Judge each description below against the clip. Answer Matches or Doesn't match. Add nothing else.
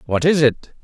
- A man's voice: Matches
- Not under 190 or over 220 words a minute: Matches